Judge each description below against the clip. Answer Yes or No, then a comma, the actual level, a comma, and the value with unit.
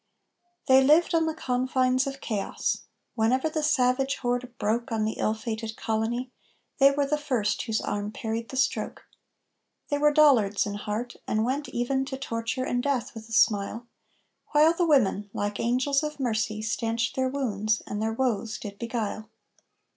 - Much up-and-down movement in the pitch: No, average, 3.7 semitones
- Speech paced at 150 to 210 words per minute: Yes, average, 170 wpm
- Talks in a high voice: Yes, high, 245 Hz